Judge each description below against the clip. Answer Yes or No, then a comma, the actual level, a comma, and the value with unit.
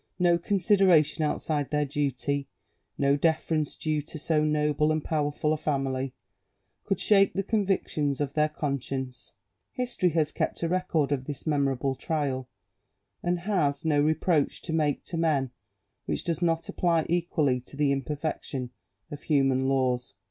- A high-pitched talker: No, medium, 150 Hz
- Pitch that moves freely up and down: No, average, 3.0 semitones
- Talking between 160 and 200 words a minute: No, average, 150 wpm